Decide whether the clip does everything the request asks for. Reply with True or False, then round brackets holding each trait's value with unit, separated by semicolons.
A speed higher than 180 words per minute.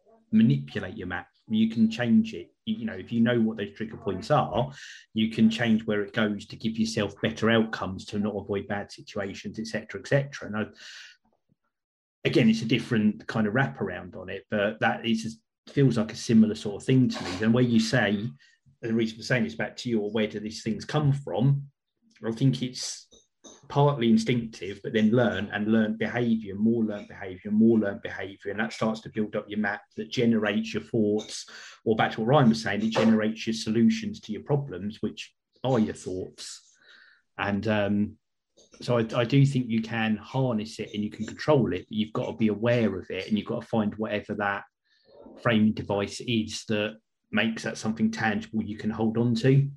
True (200 wpm)